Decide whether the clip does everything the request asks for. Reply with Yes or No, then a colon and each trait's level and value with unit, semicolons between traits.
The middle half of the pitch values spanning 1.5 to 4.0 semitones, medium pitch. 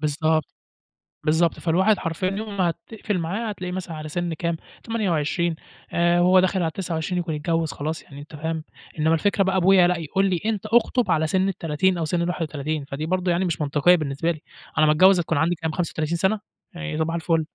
Yes: average, 2.9 semitones; medium, 170 Hz